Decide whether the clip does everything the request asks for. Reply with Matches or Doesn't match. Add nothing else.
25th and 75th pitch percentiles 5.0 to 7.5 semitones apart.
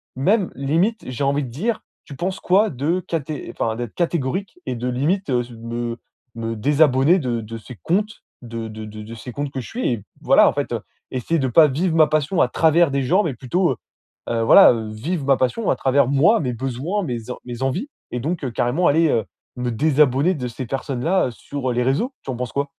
Matches